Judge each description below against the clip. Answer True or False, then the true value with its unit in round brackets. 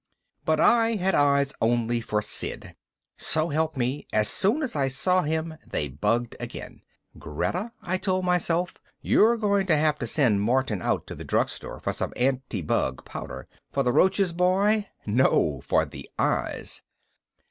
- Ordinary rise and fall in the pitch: False (7.4 semitones)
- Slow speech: False (160 wpm)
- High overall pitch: False (155 Hz)